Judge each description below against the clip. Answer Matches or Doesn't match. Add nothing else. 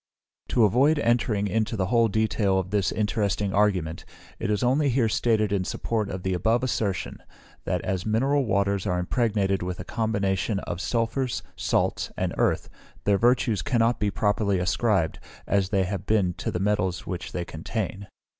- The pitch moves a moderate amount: Matches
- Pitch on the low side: Matches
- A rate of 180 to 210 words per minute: Doesn't match